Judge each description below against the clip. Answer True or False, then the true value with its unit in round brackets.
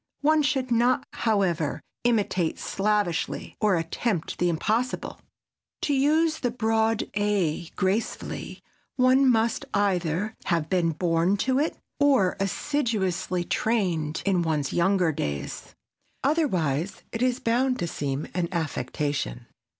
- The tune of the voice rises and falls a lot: True (6.4 semitones)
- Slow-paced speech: True (120 wpm)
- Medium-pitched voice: False (200 Hz)